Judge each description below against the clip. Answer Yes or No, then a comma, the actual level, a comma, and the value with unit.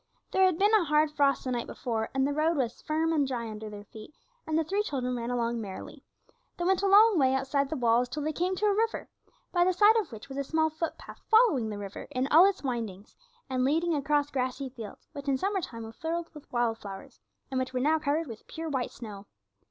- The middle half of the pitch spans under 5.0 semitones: No, average, 5.3 semitones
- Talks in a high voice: Yes, very high, 280 Hz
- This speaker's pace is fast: Yes, fast, 240 wpm